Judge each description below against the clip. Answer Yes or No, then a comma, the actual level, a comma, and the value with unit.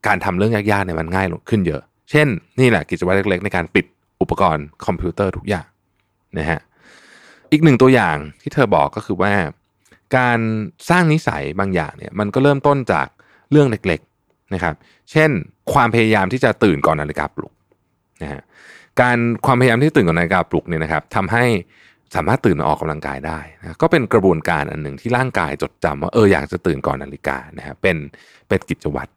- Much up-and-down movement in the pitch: Yes, wide, 6.9 semitones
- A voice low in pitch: Yes, low, 100 Hz